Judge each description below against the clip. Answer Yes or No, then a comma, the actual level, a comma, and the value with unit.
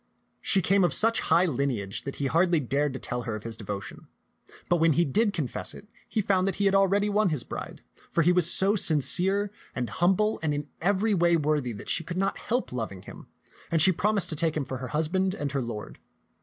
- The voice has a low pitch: No, medium, 165 Hz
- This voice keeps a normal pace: No, fast, 225 wpm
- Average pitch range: No, wide, 5.9 semitones